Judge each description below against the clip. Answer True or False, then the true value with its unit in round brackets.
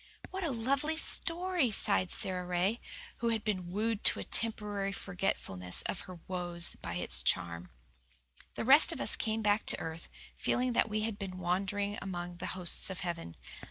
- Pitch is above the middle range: True (195 Hz)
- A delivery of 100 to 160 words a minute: False (175 wpm)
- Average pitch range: True (4.1 semitones)